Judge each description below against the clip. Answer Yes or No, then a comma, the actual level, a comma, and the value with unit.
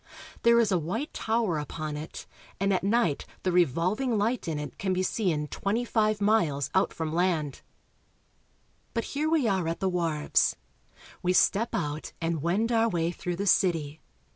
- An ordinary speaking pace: Yes, average, 170 wpm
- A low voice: No, medium, 185 Hz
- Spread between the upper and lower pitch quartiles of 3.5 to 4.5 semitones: No, average, 5.2 semitones